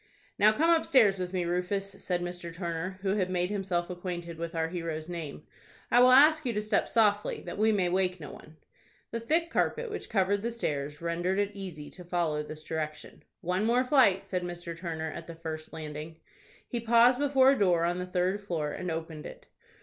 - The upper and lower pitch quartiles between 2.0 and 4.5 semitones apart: Yes, average, 4.0 semitones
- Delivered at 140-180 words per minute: No, fast, 205 wpm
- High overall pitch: No, medium, 180 Hz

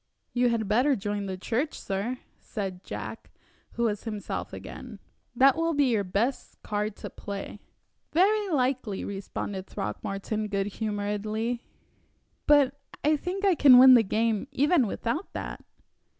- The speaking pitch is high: Yes, high, 230 Hz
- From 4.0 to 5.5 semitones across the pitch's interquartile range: Yes, average, 5.1 semitones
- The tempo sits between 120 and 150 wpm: Yes, average, 140 wpm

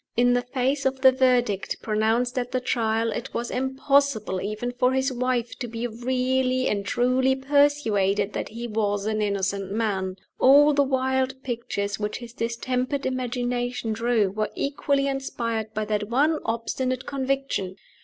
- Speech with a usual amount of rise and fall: Yes, average, 3.2 semitones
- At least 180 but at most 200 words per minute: No, average, 155 wpm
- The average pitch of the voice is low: No, high, 245 Hz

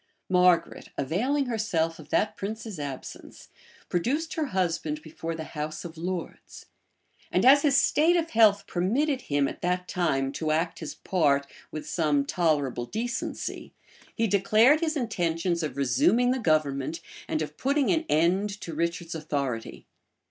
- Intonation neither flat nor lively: No, wide, 6.7 semitones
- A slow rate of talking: No, average, 150 wpm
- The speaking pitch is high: No, medium, 175 Hz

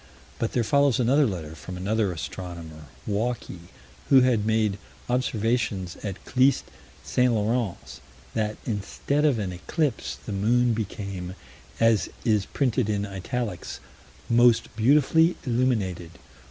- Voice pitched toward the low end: Yes, low, 110 Hz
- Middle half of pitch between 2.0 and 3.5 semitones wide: No, average, 4.2 semitones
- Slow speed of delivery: Yes, slow, 120 wpm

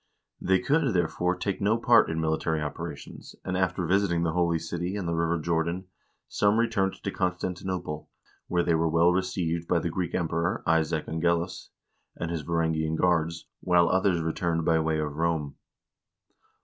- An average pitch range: No, narrow, 2.1 semitones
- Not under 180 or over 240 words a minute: No, average, 165 wpm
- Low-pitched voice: Yes, very low, 85 Hz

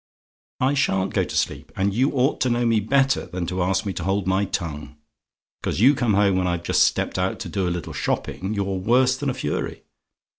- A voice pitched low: Yes, low, 100 Hz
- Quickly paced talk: Yes, fast, 225 wpm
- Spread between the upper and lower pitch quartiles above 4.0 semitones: Yes, average, 5.1 semitones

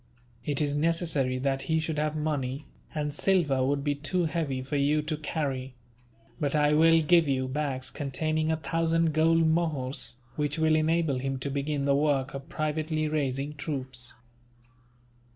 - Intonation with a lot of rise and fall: No, narrow, 2.5 semitones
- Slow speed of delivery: No, average, 160 wpm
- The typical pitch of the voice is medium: Yes, medium, 150 Hz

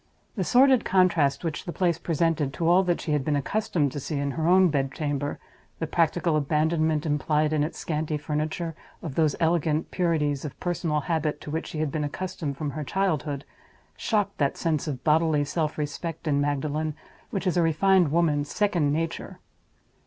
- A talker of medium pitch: Yes, medium, 155 Hz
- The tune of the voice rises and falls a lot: No, narrow, 2.6 semitones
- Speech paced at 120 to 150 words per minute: No, average, 175 wpm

